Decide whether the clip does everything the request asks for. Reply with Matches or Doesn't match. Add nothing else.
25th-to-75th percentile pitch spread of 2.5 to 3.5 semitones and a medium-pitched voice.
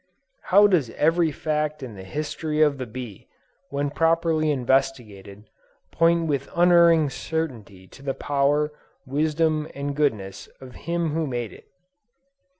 Doesn't match